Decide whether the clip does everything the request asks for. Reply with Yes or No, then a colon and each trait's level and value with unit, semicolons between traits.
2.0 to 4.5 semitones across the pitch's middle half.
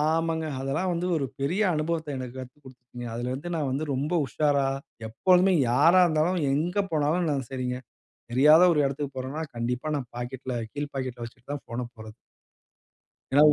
Yes: average, 3.9 semitones